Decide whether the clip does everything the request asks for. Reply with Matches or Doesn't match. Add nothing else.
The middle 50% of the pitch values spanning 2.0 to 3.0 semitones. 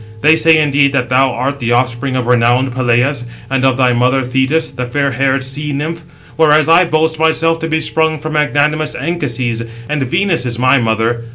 Doesn't match